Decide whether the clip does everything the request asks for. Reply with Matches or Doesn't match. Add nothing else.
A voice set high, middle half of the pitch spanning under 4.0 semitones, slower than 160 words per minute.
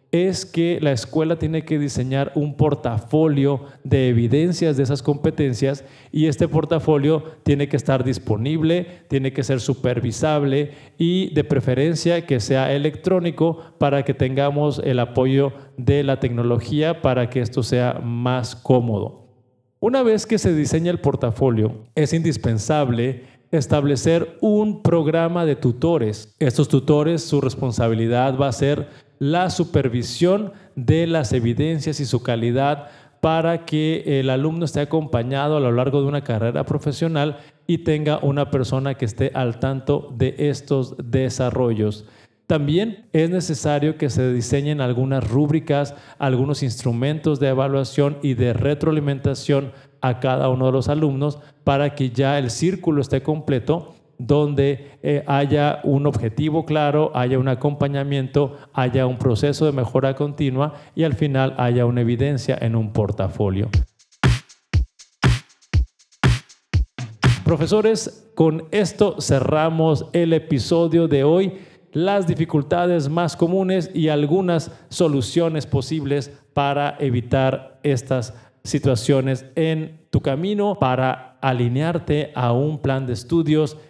Doesn't match